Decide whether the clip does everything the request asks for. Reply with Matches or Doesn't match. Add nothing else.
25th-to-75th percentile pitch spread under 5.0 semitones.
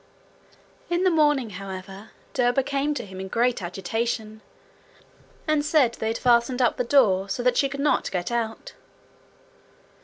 Doesn't match